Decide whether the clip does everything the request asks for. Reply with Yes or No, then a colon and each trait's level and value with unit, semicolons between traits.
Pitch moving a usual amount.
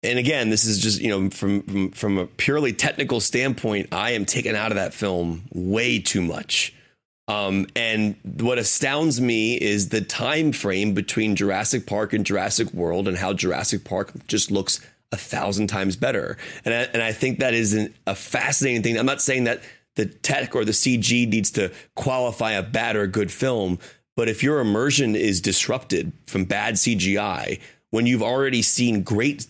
Yes: average, 3.5 semitones